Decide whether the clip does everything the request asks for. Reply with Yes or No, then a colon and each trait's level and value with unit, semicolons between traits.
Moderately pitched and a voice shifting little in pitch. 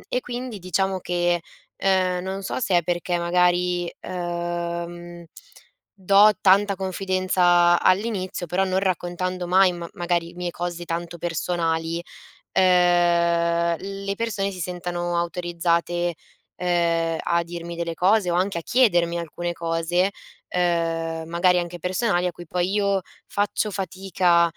Yes: medium, 175 Hz; narrow, 1.5 semitones